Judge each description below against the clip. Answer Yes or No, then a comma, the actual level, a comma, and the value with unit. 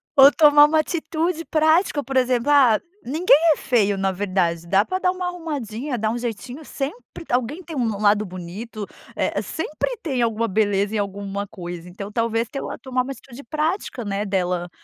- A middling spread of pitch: No, wide, 6.6 semitones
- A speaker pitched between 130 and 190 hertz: No, high, 240 Hz